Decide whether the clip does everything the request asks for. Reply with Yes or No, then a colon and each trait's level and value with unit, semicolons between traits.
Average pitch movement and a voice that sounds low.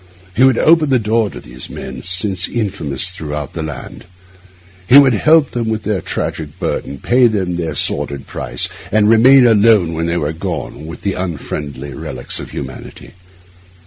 No: wide, 6.4 semitones; very low, 95 Hz